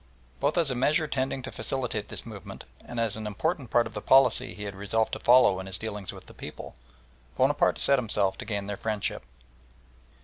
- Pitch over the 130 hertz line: No, low, 110 Hz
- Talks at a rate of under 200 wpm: No, fast, 205 wpm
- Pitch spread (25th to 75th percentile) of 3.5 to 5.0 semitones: Yes, average, 4.3 semitones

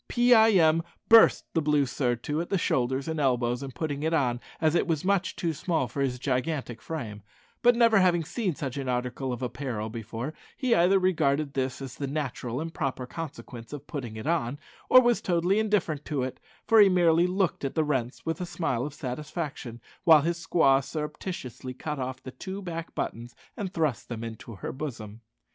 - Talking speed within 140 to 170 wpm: No, average, 195 wpm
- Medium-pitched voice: Yes, medium, 150 Hz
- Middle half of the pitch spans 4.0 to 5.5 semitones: Yes, average, 5.2 semitones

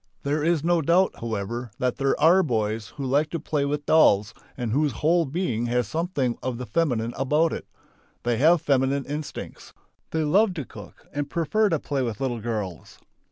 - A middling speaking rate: Yes, average, 185 wpm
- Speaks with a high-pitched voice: No, medium, 140 Hz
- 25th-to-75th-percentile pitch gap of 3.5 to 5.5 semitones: Yes, average, 5.1 semitones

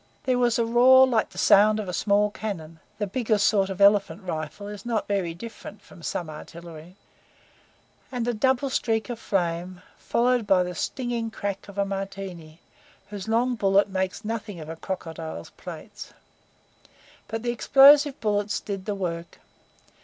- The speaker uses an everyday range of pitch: Yes, average, 4.0 semitones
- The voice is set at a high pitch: Yes, high, 205 Hz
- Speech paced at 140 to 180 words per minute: Yes, average, 160 wpm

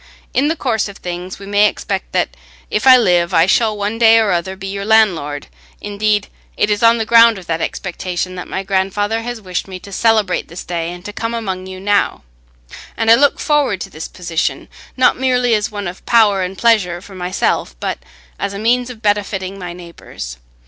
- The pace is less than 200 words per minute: No, fast, 205 wpm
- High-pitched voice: Yes, high, 200 Hz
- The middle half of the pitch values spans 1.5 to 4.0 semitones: Yes, average, 3.6 semitones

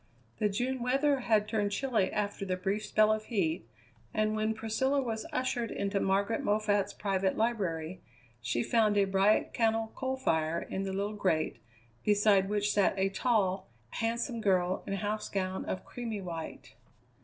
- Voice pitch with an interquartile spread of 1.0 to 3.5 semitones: Yes, average, 2.8 semitones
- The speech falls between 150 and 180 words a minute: Yes, average, 160 wpm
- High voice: Yes, high, 210 Hz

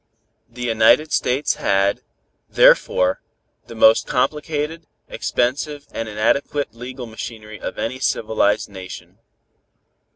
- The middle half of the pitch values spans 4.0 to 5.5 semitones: Yes, average, 4.6 semitones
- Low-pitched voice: Yes, low, 120 Hz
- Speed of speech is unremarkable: No, slow, 100 wpm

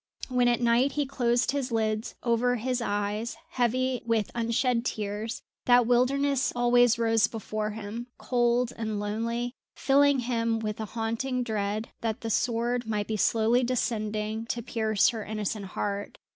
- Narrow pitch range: Yes, narrow, 2.2 semitones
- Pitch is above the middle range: Yes, high, 230 Hz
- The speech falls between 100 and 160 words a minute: Yes, average, 150 wpm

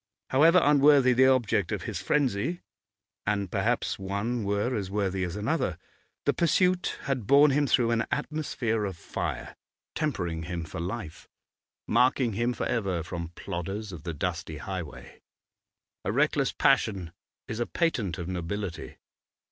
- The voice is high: No, low, 105 Hz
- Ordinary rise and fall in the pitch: No, wide, 6.4 semitones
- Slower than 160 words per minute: Yes, average, 145 wpm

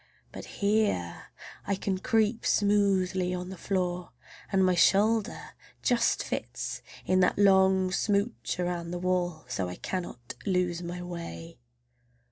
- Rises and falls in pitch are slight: Yes, narrow, 2.3 semitones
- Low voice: No, medium, 185 Hz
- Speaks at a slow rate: Yes, slow, 130 wpm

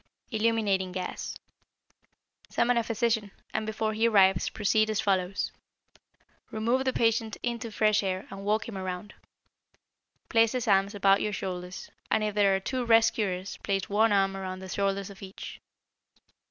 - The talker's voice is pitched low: No, high, 205 Hz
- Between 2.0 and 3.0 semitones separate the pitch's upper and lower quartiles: Yes, narrow, 2.4 semitones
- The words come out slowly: No, average, 155 wpm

